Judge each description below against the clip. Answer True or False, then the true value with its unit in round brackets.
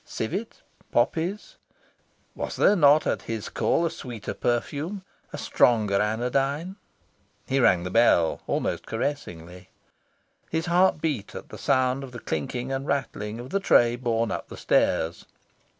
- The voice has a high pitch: False (125 Hz)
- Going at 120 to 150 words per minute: True (140 wpm)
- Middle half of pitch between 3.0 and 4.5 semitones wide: False (5.4 semitones)